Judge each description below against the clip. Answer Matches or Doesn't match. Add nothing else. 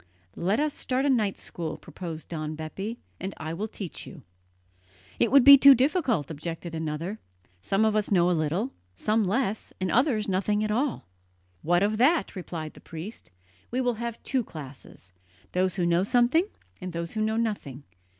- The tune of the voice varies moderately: Doesn't match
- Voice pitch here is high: Matches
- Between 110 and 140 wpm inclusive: Doesn't match